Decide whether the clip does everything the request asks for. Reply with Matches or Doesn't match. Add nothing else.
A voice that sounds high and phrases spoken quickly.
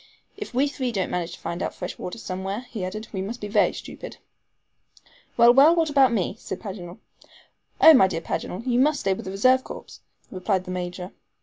Matches